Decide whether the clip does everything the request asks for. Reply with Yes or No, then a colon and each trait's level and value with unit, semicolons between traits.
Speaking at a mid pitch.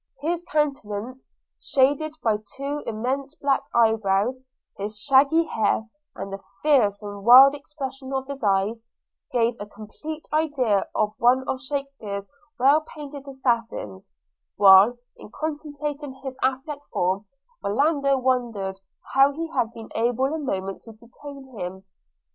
No: very high, 260 Hz